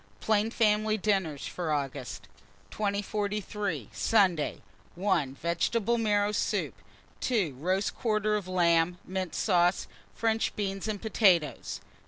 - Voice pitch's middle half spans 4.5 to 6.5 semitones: No, average, 3.9 semitones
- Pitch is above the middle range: Yes, high, 195 Hz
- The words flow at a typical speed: No, slow, 110 wpm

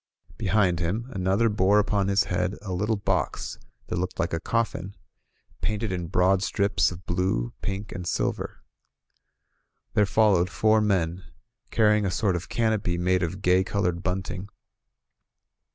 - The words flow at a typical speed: Yes, average, 150 wpm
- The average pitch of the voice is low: Yes, very low, 95 Hz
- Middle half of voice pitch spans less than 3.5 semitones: Yes, narrow, 2.6 semitones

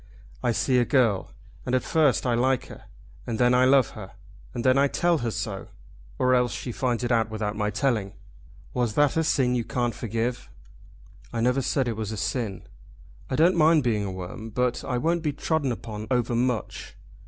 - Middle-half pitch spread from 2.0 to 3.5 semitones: Yes, average, 2.9 semitones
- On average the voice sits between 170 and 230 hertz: No, low, 125 Hz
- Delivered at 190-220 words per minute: Yes, average, 195 wpm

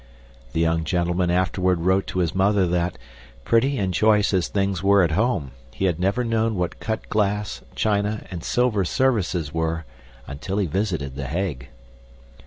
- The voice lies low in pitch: Yes, very low, 95 Hz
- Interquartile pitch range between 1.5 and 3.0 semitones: No, average, 3.6 semitones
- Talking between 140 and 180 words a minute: Yes, average, 165 wpm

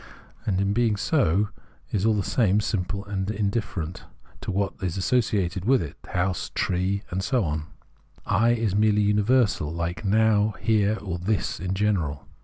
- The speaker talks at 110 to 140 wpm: No, average, 170 wpm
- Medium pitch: No, low, 100 Hz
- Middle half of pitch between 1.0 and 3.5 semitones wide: Yes, average, 2.8 semitones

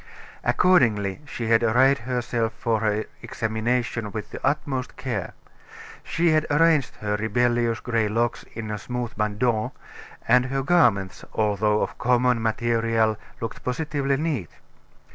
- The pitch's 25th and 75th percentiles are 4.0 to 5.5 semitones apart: No, average, 2.7 semitones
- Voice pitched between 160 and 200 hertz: No, low, 115 Hz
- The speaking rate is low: Yes, slow, 125 wpm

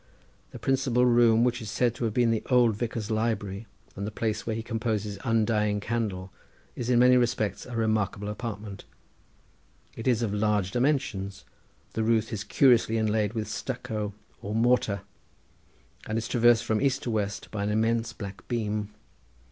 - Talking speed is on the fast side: No, average, 170 wpm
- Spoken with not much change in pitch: Yes, narrow, 2.3 semitones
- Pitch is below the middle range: Yes, low, 110 Hz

